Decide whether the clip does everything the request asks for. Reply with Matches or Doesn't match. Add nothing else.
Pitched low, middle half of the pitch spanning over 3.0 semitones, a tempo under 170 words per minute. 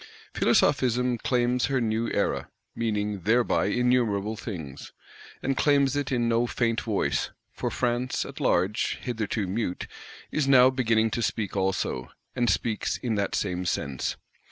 Matches